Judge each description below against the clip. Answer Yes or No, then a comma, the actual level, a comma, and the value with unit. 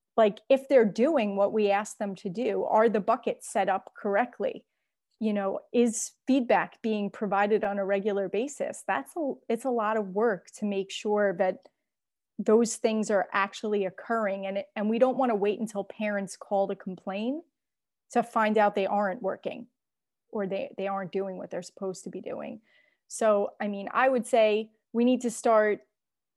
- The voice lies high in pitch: Yes, high, 215 Hz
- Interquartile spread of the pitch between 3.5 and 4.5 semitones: No, average, 3.0 semitones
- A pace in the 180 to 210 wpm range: Yes, average, 185 wpm